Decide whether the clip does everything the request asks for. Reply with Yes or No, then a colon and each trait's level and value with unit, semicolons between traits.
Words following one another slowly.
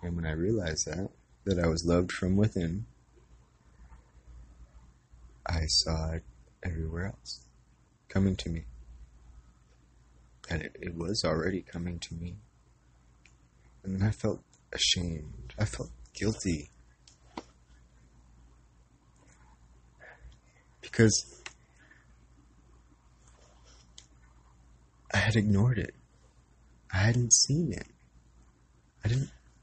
Yes: slow, 95 wpm